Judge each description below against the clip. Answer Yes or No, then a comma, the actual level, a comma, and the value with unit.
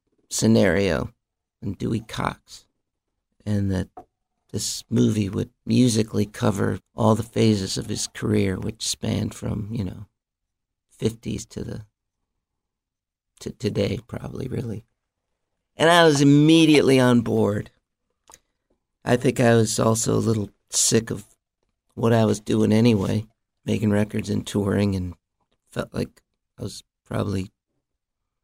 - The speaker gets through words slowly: Yes, slow, 125 wpm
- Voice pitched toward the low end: Yes, low, 110 Hz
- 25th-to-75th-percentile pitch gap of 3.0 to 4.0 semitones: No, narrow, 2.5 semitones